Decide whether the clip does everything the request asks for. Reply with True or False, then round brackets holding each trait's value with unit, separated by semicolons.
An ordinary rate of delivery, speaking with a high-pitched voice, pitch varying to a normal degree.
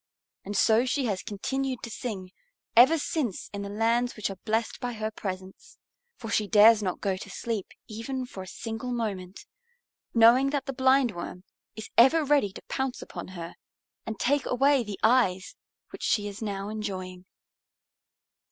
True (165 wpm; 220 Hz; 4.0 semitones)